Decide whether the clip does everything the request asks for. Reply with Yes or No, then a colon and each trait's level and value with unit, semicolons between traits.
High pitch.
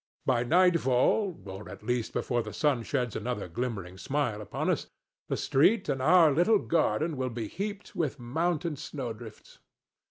No: low, 130 Hz